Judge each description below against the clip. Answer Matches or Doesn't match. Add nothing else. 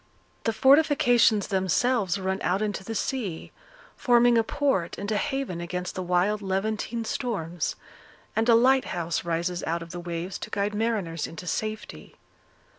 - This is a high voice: Matches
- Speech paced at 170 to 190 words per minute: Doesn't match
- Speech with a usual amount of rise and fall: Matches